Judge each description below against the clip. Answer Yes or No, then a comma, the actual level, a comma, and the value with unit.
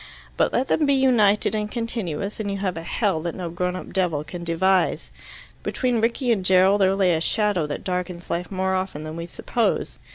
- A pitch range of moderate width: Yes, average, 3.5 semitones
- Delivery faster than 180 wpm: Yes, fast, 205 wpm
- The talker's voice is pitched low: No, high, 190 Hz